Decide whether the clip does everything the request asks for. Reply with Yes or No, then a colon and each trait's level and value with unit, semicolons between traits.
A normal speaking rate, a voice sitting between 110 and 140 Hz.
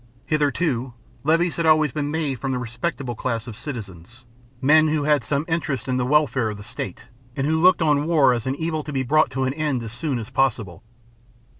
No: fast, 210 wpm; low, 135 Hz